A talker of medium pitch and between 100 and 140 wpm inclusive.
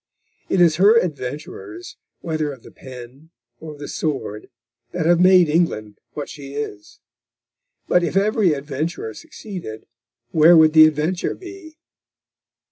Yes: medium, 155 Hz; slow, 135 wpm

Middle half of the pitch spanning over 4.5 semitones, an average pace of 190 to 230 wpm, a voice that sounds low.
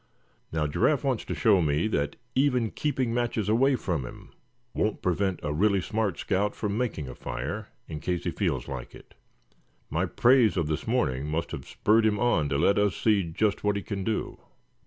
Yes: wide, 5.5 semitones; average, 195 wpm; low, 100 Hz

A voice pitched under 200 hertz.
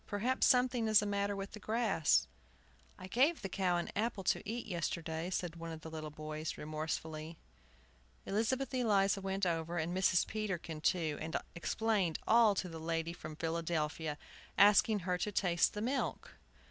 Yes: medium, 185 Hz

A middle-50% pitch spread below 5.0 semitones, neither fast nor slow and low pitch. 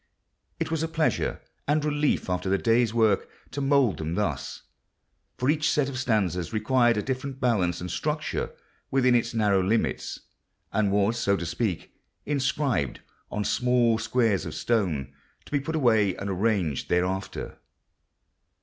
No: wide, 5.6 semitones; average, 150 wpm; low, 115 Hz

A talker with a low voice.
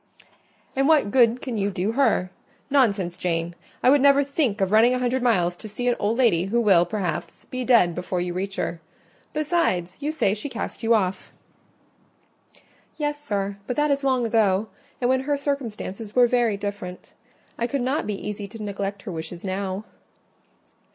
No: high, 220 Hz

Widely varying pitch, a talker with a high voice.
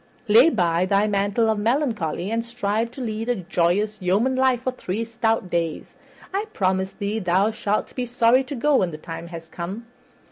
No: average, 4.3 semitones; high, 215 Hz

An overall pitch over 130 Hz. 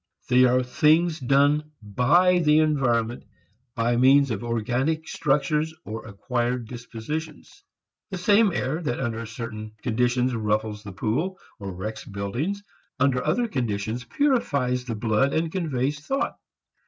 No: low, 125 Hz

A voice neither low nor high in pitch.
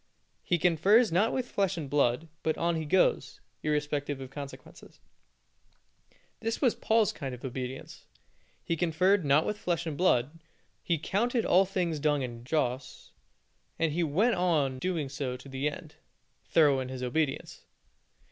Yes: medium, 155 Hz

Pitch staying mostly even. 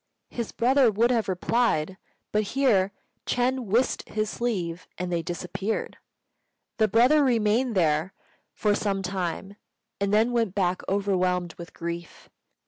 No: average, 4.5 semitones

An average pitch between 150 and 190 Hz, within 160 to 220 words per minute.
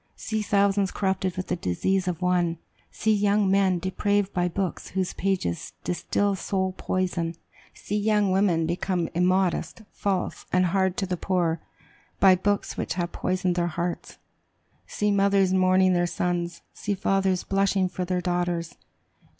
No: medium, 185 Hz; average, 150 wpm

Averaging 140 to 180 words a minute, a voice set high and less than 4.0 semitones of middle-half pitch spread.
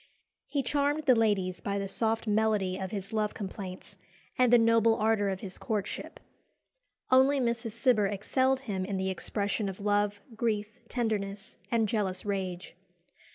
Yes: average, 155 wpm; high, 210 Hz; average, 2.7 semitones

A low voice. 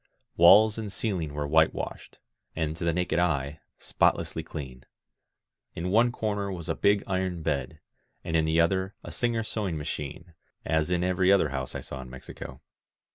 Yes: very low, 85 Hz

